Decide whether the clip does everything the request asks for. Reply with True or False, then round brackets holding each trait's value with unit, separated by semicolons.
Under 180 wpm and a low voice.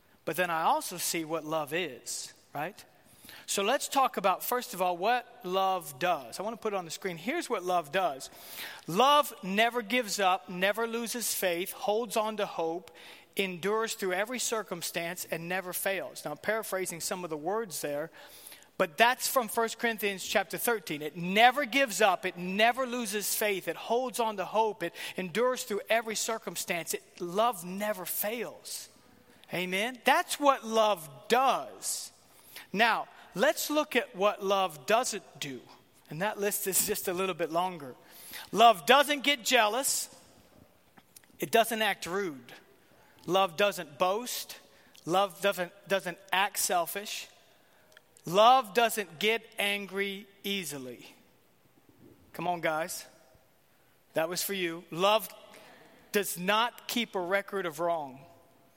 False (145 wpm; 200 Hz)